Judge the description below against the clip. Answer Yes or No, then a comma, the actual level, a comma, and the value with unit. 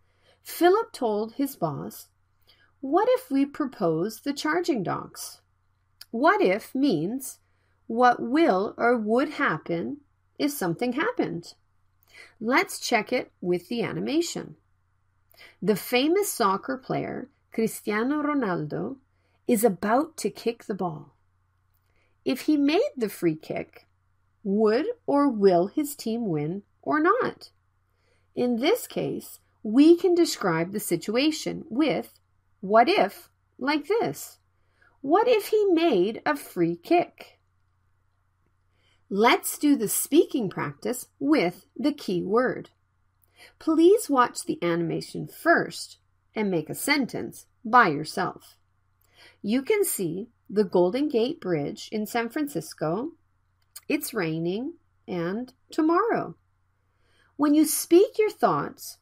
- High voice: Yes, high, 230 Hz